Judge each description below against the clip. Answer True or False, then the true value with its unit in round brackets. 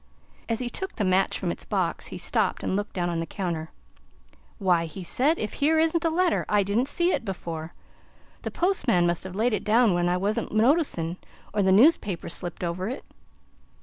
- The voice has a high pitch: True (205 Hz)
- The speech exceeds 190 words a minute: True (200 wpm)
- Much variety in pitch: True (6.5 semitones)